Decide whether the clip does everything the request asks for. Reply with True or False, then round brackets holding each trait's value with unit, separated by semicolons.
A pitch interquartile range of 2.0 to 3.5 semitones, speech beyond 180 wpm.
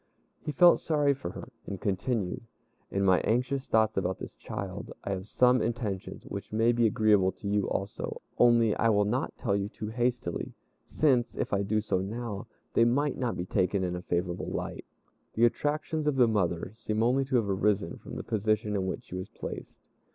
False (3.9 semitones; 195 wpm)